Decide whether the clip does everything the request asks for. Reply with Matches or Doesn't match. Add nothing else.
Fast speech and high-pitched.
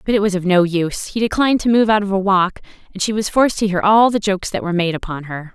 Matches